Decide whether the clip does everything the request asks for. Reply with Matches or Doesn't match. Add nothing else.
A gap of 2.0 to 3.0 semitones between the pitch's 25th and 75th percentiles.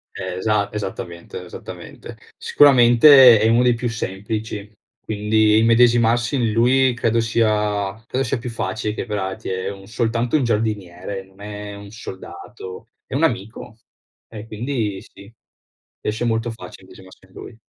Matches